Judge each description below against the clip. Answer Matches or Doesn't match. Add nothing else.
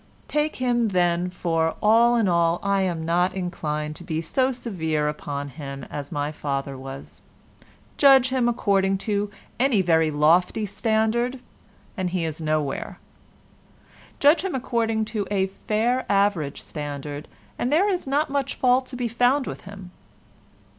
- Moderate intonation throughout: Doesn't match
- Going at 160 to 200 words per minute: Doesn't match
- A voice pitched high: Matches